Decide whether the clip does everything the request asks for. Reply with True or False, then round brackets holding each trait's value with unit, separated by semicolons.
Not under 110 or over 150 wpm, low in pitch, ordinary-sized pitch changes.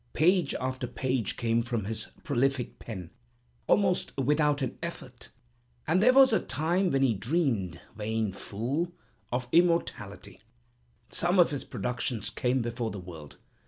False (140 wpm; 130 Hz; 6.3 semitones)